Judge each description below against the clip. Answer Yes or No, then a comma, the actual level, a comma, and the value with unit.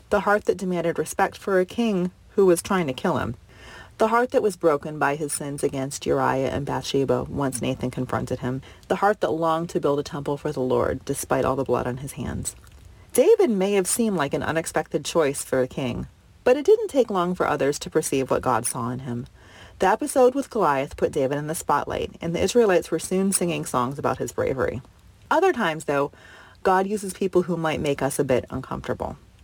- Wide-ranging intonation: Yes, wide, 6.4 semitones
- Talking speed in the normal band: No, fast, 215 wpm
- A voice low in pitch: No, medium, 160 Hz